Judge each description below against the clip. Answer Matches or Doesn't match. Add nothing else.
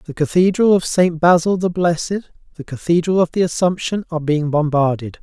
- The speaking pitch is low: Doesn't match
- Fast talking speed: Doesn't match